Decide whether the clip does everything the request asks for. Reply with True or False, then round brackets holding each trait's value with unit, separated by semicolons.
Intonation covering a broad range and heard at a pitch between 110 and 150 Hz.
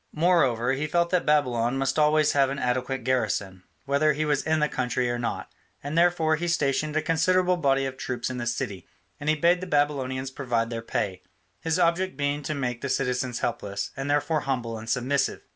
False (3.8 semitones; 140 Hz)